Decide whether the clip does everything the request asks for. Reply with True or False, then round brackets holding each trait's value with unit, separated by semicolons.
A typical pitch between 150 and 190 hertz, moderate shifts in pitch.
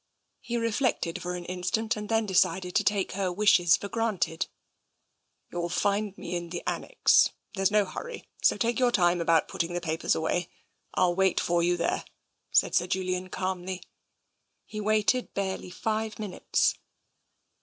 True (185 Hz; 3.3 semitones)